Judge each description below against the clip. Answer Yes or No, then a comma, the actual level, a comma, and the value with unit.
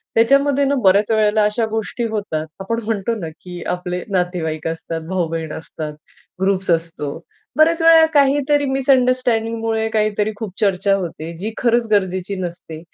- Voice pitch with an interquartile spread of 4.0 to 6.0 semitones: Yes, average, 4.8 semitones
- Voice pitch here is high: Yes, high, 210 Hz